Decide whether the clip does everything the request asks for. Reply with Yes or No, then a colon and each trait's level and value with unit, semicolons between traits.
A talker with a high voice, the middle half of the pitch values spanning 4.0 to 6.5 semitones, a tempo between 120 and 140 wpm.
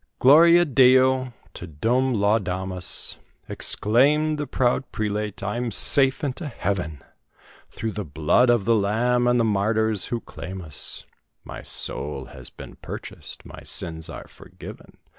No: low, 115 Hz; average, 5.0 semitones; slow, 135 wpm